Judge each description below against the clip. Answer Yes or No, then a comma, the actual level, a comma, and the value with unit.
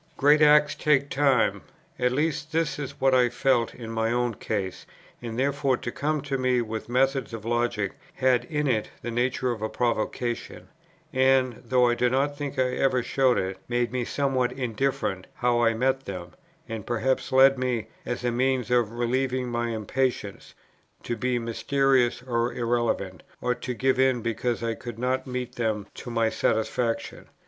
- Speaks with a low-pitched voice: Yes, low, 125 Hz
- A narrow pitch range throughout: Yes, narrow, 2.2 semitones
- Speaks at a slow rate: No, average, 175 wpm